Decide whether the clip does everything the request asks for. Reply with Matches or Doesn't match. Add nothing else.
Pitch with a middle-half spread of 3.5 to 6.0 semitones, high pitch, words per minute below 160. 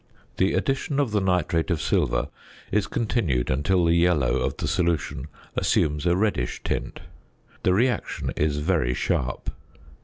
Doesn't match